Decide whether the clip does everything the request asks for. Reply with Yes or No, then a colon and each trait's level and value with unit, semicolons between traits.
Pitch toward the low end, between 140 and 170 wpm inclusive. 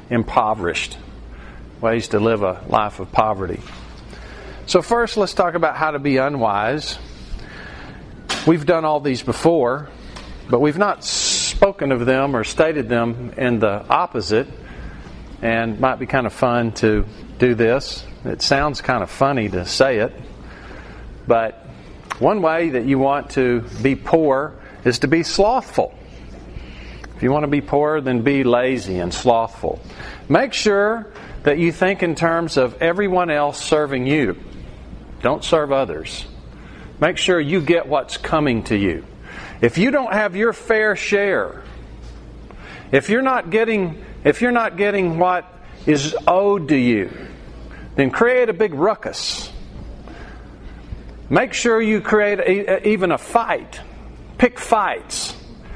No: medium, 145 Hz; average, 145 wpm